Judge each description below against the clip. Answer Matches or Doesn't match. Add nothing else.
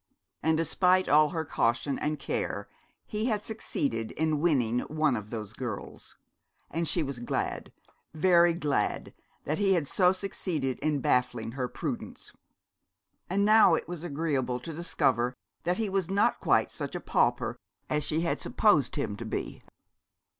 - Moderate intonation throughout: Doesn't match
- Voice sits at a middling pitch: Matches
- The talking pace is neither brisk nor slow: Matches